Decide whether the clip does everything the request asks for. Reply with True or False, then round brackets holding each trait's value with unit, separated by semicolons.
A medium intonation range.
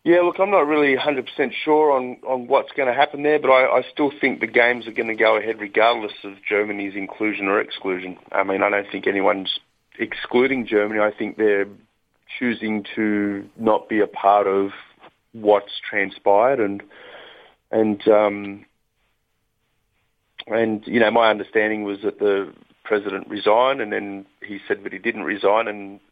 True (3.2 semitones)